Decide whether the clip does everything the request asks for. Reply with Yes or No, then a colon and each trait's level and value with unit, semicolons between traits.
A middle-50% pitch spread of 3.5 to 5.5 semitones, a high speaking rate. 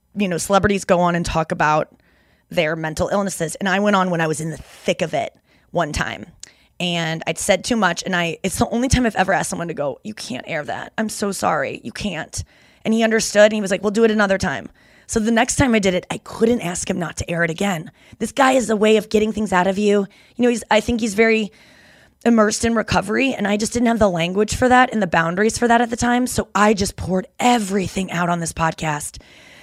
Yes: average, 4.2 semitones; fast, 255 wpm